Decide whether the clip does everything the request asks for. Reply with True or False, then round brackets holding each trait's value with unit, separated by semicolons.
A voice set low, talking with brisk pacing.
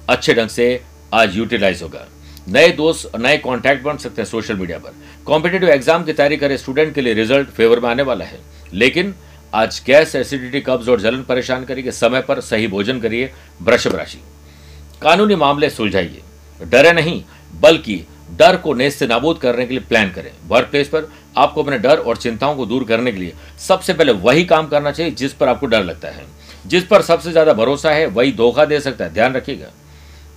True (125 Hz; 200 wpm)